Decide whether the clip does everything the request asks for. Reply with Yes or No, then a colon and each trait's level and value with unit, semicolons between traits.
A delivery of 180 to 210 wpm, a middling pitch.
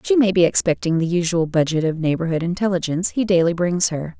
Yes: average, 200 wpm; medium, 175 Hz